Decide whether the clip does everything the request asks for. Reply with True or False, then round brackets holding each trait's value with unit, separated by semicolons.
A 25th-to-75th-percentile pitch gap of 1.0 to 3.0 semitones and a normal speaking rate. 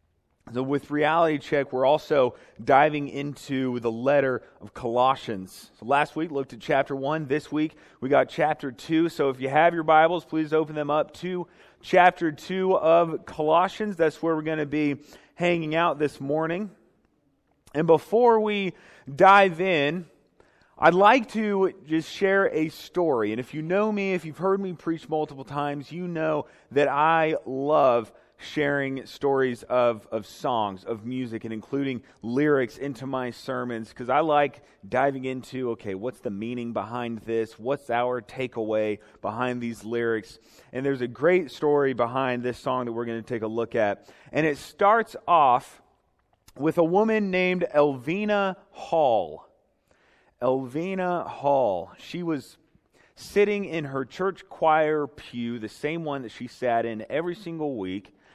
False (4.8 semitones; 160 wpm)